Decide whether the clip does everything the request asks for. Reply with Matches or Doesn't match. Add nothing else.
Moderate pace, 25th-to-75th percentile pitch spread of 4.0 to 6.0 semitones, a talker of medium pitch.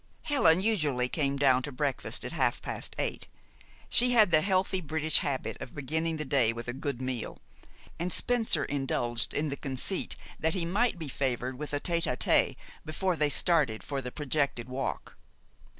Matches